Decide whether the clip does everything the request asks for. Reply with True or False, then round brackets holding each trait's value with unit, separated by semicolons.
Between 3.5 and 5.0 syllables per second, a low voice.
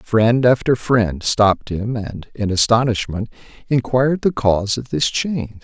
True (4.5 syllables/s; 115 Hz)